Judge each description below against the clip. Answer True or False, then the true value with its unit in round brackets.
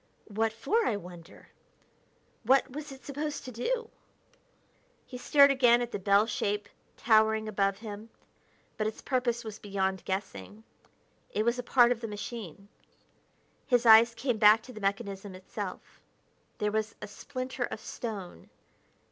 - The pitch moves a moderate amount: True (3.3 semitones)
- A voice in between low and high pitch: False (220 Hz)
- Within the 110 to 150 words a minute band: True (145 wpm)